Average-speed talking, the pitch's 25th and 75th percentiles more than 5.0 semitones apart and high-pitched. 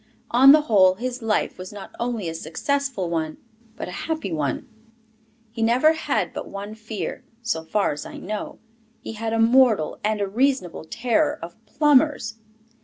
Yes: average, 170 wpm; wide, 5.6 semitones; high, 225 Hz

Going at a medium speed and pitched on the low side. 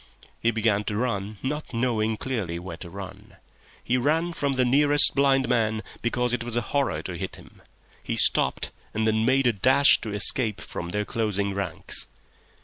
Yes: average, 175 wpm; low, 115 Hz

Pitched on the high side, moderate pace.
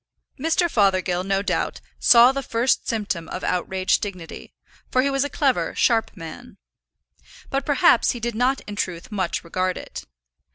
Yes: high, 215 Hz; average, 160 wpm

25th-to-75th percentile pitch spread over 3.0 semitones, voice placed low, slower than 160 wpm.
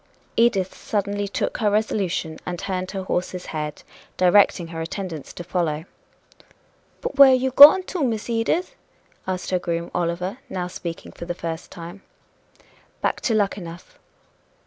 No: average, 3.8 semitones; medium, 185 Hz; average, 150 wpm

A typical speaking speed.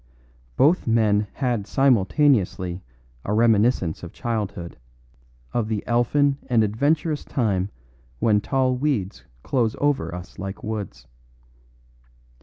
No: slow, 105 wpm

